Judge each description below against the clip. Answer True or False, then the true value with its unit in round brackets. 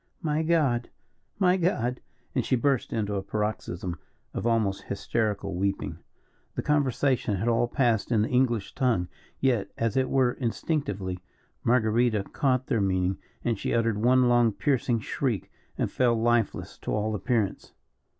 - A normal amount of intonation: True (3.7 semitones)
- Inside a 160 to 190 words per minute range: False (150 wpm)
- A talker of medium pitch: False (115 Hz)